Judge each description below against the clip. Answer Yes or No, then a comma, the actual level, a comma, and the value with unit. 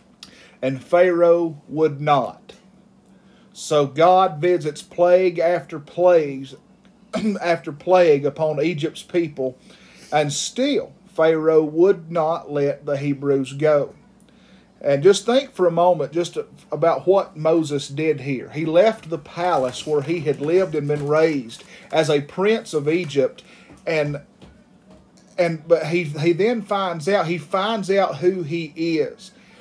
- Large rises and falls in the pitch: No, average, 3.9 semitones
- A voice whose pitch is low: No, medium, 170 Hz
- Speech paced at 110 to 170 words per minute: Yes, slow, 135 wpm